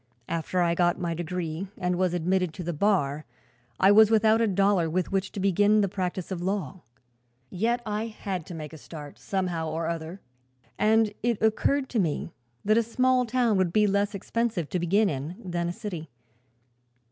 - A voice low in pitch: No, medium, 185 Hz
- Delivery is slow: No, average, 185 wpm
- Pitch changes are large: No, average, 3.8 semitones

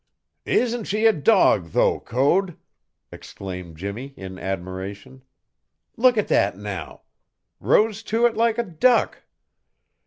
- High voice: No, low, 135 Hz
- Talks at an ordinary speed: No, slow, 120 wpm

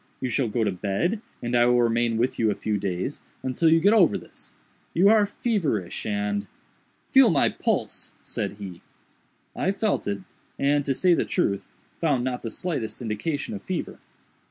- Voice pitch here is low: Yes, low, 125 Hz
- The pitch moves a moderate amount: No, wide, 8.1 semitones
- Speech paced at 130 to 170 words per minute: No, average, 180 wpm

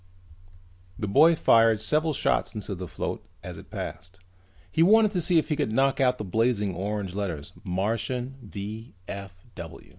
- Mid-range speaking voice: No, low, 110 Hz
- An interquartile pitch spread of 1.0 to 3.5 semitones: No, wide, 5.6 semitones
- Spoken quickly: No, average, 155 wpm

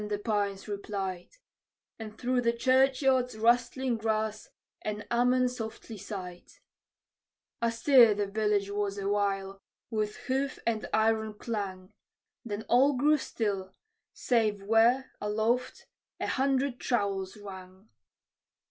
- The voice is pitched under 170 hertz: No, high, 220 Hz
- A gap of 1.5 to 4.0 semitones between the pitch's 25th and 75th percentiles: Yes, average, 3.4 semitones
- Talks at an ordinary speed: No, slow, 110 wpm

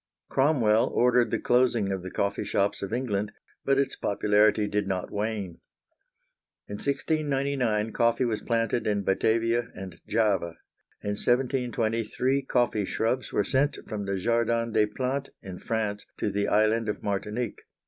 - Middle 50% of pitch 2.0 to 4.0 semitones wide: Yes, average, 3.2 semitones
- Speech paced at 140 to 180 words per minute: Yes, average, 150 wpm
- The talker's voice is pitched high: No, low, 110 Hz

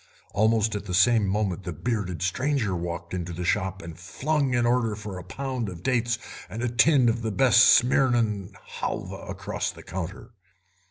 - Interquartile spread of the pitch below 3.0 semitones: No, average, 4.8 semitones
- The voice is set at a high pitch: No, low, 110 Hz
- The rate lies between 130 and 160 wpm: No, average, 175 wpm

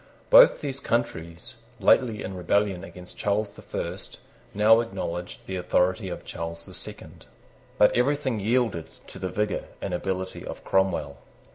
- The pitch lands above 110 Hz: No, low, 100 Hz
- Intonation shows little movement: No, average, 4.2 semitones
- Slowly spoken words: No, average, 145 wpm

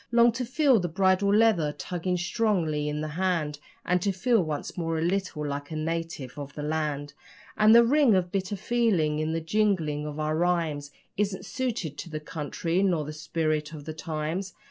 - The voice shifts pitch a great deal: No, average, 4.5 semitones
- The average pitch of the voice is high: No, medium, 165 Hz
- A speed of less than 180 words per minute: No, average, 190 wpm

